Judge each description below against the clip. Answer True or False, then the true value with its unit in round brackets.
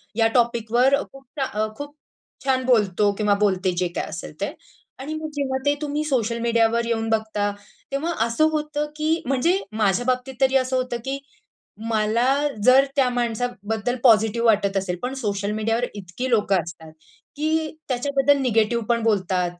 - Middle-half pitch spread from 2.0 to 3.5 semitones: False (4.1 semitones)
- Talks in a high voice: True (235 Hz)